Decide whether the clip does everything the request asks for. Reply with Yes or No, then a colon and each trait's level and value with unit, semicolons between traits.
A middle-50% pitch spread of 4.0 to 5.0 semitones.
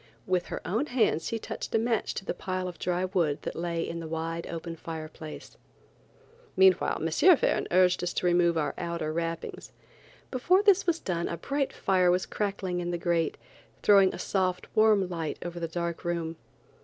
No: average, 2.7 semitones